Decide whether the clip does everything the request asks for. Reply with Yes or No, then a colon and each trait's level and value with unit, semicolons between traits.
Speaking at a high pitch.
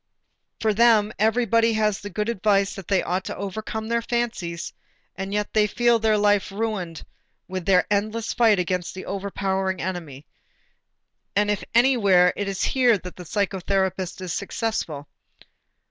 Yes: high, 200 Hz